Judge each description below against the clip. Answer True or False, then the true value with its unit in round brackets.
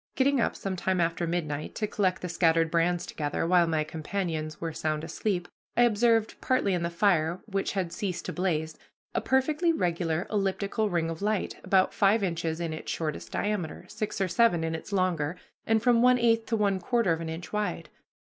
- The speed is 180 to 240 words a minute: True (195 wpm)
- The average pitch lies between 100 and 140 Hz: False (180 Hz)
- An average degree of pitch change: True (4.2 semitones)